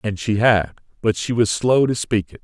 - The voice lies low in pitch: Yes, low, 105 Hz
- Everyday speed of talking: No, fast, 245 wpm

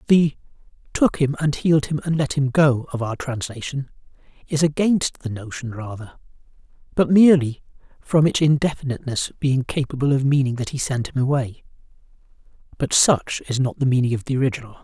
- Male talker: Yes, male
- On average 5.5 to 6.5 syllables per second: Yes, 5.6 syllables/s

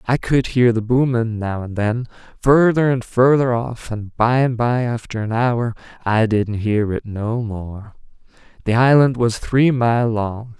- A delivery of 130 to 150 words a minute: No, average, 175 wpm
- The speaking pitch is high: No, low, 120 Hz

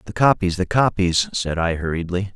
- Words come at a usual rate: Yes, average, 180 wpm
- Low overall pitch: Yes, very low, 90 Hz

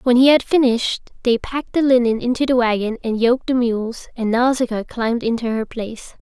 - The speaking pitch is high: Yes, high, 240 Hz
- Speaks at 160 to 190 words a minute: No, average, 200 wpm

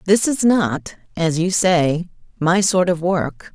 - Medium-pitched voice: Yes, medium, 180 Hz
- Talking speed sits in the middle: Yes, average, 170 wpm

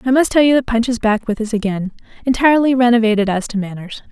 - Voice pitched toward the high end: Yes, high, 230 Hz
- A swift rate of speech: Yes, fast, 235 wpm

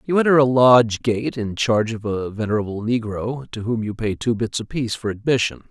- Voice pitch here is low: Yes, low, 115 Hz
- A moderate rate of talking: No, fast, 210 wpm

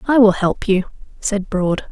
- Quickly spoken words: No, average, 190 wpm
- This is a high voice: Yes, high, 200 Hz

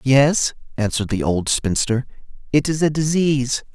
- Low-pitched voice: Yes, low, 130 Hz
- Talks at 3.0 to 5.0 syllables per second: Yes, 4.9 syllables/s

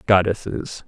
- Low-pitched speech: Yes, very low, 95 Hz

